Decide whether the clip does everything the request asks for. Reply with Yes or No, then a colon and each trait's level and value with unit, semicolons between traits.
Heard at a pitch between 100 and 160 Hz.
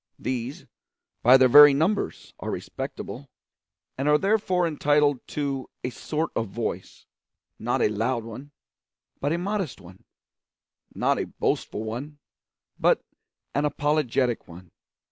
Yes: medium, 140 Hz